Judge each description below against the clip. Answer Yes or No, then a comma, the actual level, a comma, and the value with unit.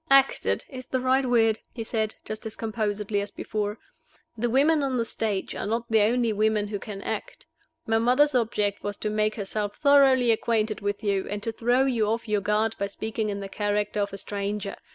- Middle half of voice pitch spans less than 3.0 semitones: Yes, narrow, 2.5 semitones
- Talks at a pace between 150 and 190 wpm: No, fast, 205 wpm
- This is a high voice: Yes, high, 220 Hz